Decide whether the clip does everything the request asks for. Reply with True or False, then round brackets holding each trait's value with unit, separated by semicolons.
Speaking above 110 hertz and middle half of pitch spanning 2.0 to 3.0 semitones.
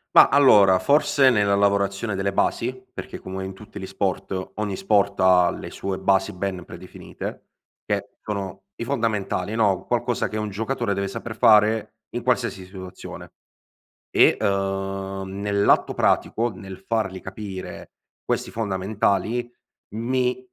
False (100 Hz; 2.5 semitones)